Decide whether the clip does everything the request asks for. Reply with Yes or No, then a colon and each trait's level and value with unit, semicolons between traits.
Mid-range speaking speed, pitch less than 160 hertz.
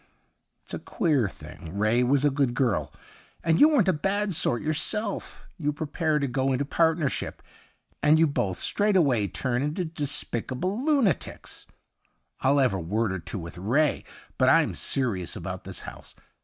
Yes: average, 165 wpm; medium, 140 Hz